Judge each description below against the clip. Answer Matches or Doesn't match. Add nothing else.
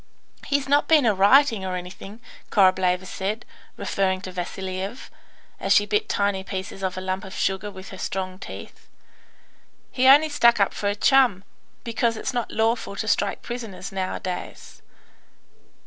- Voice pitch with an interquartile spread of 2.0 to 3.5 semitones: Doesn't match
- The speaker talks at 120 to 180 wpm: Matches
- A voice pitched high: Matches